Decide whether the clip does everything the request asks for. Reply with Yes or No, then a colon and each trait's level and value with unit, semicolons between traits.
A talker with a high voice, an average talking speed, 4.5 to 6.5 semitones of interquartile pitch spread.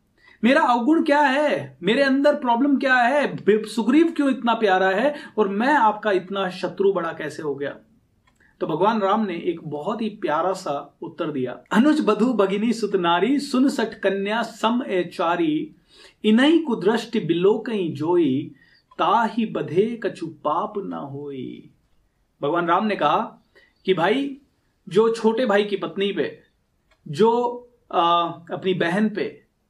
Yes: high, 210 Hz; average, 145 wpm; average, 4.9 semitones